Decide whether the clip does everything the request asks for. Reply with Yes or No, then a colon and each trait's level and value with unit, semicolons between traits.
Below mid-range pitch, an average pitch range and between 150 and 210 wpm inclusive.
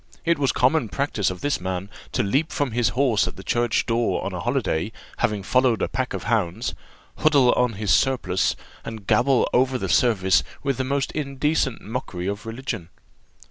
Yes: low, 120 Hz; average, 4.7 semitones; average, 185 wpm